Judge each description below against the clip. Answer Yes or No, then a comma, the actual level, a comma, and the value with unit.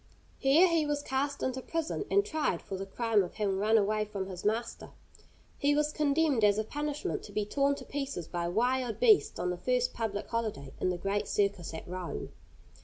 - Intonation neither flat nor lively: No, wide, 6.4 semitones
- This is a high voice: Yes, high, 225 Hz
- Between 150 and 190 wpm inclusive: No, average, 200 wpm